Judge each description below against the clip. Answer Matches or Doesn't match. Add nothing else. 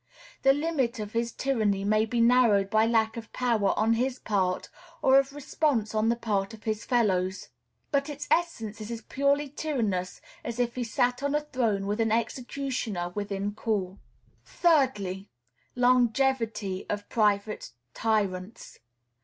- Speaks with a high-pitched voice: Matches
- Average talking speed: Matches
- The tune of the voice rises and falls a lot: Doesn't match